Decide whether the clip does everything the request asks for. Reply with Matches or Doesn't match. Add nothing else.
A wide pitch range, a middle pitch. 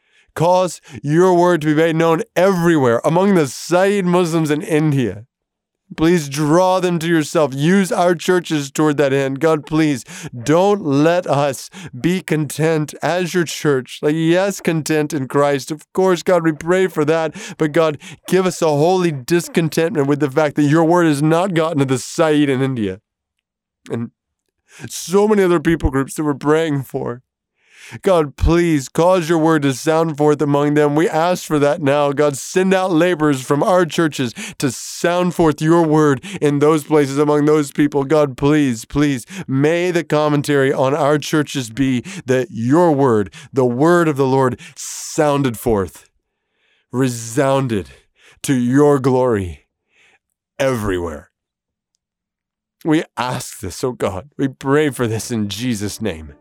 Doesn't match